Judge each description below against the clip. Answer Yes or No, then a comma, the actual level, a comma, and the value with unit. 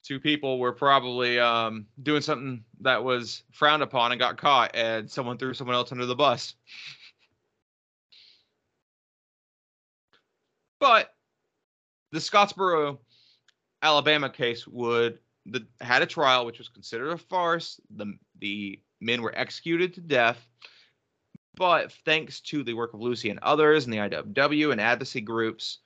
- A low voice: Yes, low, 125 Hz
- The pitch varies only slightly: No, average, 4.4 semitones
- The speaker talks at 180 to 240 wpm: No, slow, 135 wpm